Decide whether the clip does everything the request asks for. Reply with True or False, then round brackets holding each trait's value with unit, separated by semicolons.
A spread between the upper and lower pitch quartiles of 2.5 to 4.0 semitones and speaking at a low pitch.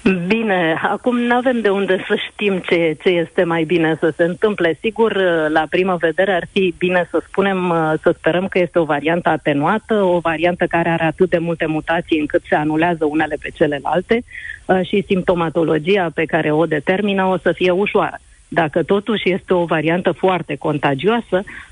False (3.0 semitones; 175 Hz)